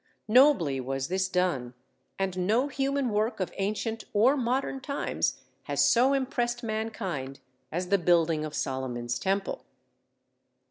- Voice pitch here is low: No, high, 195 Hz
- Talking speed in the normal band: No, slow, 130 wpm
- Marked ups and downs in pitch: Yes, wide, 7.1 semitones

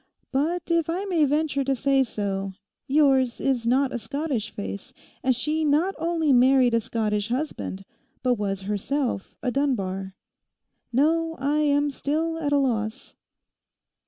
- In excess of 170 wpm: No, average, 145 wpm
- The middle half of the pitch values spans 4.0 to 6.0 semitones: Yes, average, 4.8 semitones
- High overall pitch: Yes, very high, 270 Hz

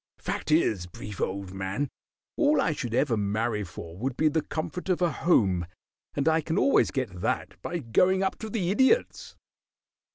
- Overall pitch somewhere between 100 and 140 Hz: Yes, low, 135 Hz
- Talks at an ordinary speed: Yes, average, 175 wpm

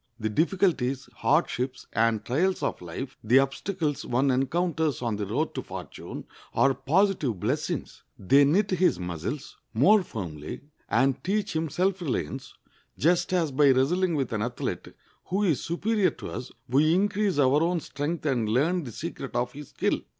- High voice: No, medium, 145 Hz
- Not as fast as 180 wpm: Yes, average, 155 wpm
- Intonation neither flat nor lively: No, wide, 6.0 semitones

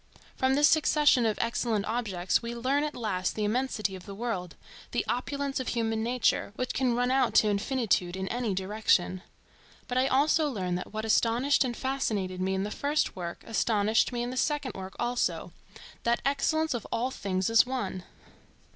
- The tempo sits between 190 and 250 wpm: No, average, 180 wpm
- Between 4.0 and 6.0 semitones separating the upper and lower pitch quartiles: Yes, average, 4.7 semitones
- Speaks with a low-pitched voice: No, high, 235 Hz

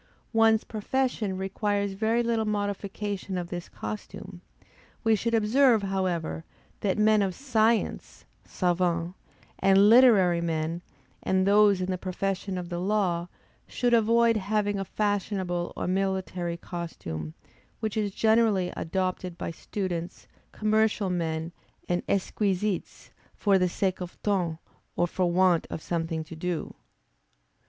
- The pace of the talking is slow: Yes, slow, 130 wpm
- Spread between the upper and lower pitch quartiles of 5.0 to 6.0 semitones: No, average, 3.2 semitones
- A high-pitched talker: Yes, high, 195 Hz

